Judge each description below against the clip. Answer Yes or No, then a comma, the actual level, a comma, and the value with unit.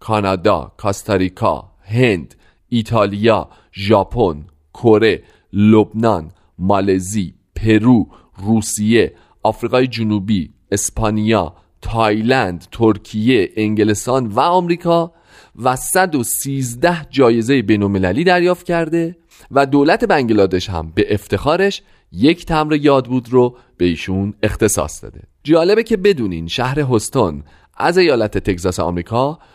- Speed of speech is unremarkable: No, slow, 95 wpm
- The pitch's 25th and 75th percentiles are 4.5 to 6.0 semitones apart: Yes, average, 5.1 semitones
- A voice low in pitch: Yes, low, 110 Hz